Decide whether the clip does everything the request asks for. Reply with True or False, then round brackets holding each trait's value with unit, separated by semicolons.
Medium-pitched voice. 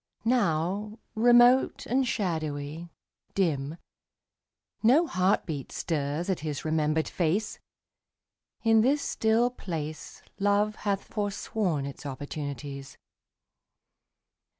True (180 Hz)